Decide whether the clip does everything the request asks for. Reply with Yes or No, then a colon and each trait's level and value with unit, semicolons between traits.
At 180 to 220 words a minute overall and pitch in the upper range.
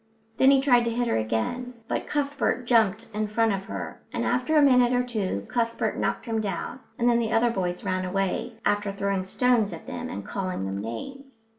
Yes: fast, 205 wpm; high, 225 Hz